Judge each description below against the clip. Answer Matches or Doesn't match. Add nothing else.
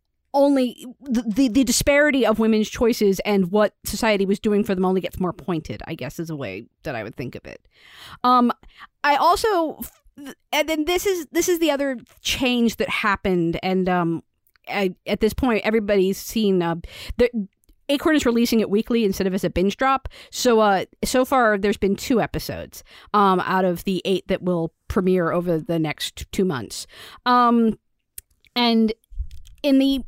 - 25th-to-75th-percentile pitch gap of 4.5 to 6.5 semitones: Matches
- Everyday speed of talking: Matches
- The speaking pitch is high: Matches